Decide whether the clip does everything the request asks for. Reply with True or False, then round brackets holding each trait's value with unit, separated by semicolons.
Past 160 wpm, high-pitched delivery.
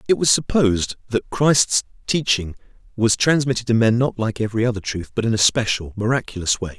False (185 wpm; 115 Hz)